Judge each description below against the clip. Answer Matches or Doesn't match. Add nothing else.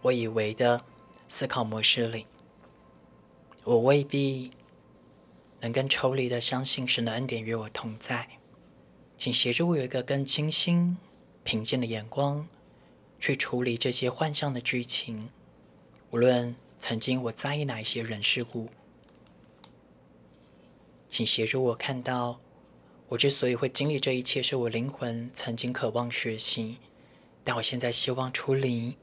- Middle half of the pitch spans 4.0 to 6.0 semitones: Doesn't match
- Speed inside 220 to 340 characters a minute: Doesn't match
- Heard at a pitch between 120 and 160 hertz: Matches